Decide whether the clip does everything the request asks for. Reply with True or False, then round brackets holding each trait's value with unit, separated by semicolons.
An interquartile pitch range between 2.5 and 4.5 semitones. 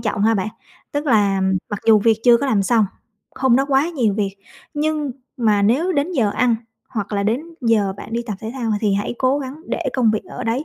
True (4.2 semitones)